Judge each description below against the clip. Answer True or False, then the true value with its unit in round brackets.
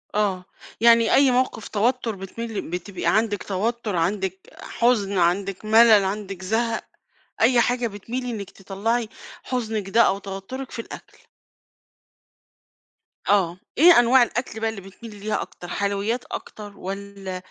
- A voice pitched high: True (210 Hz)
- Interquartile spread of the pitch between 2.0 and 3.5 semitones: True (3.1 semitones)